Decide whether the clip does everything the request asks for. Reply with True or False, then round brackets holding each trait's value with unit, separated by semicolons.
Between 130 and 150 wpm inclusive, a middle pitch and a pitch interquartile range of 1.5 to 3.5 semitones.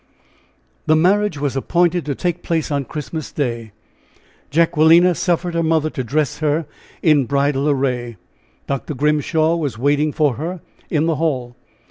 True (140 wpm; 155 Hz; 3.1 semitones)